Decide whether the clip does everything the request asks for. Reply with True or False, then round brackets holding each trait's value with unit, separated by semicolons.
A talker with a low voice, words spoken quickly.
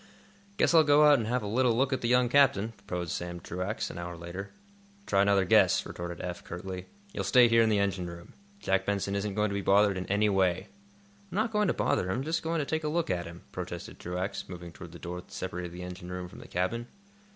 True (100 Hz; 240 wpm)